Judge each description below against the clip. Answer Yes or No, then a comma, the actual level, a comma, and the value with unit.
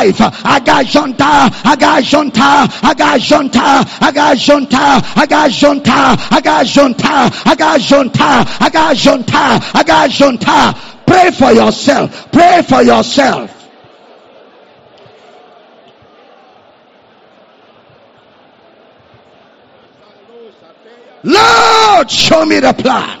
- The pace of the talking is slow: Yes, slow, 75 wpm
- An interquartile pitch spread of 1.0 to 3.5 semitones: Yes, average, 2.8 semitones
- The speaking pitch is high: Yes, very high, 285 Hz